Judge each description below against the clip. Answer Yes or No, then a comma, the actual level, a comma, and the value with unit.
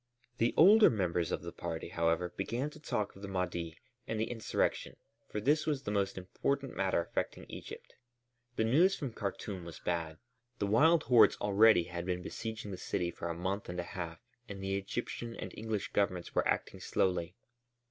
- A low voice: Yes, low, 100 Hz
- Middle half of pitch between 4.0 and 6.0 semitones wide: Yes, average, 4.6 semitones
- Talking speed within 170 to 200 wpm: Yes, average, 185 wpm